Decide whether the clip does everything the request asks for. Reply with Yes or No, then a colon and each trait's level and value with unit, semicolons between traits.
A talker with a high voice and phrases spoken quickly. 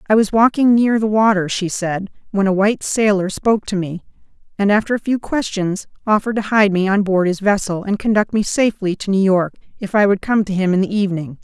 Yes: high, 200 Hz; fast, 230 wpm